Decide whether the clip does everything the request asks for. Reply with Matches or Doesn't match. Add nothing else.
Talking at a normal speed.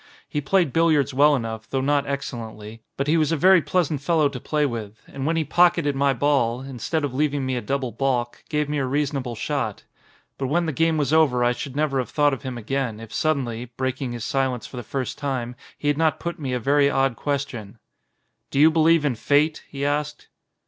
Doesn't match